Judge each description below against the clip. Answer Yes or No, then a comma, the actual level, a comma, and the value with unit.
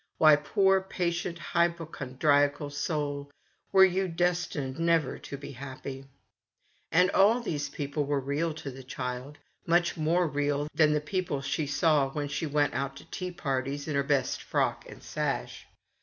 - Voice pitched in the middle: Yes, medium, 150 Hz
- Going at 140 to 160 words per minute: Yes, average, 155 wpm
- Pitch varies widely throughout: No, average, 3.4 semitones